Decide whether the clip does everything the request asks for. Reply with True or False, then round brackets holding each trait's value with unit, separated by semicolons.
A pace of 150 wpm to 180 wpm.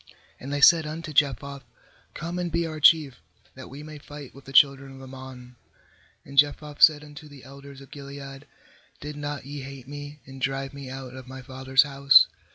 False (190 wpm)